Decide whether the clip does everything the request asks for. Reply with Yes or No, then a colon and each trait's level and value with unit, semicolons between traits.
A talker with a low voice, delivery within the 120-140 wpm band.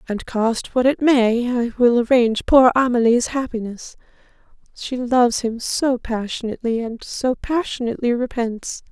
No: high, 240 Hz; slow, 135 wpm